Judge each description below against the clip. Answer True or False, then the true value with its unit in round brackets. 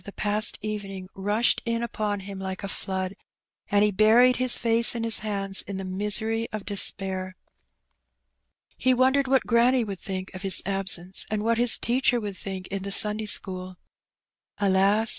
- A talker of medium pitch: False (205 Hz)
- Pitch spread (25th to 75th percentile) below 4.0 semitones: True (2.9 semitones)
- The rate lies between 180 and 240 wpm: False (170 wpm)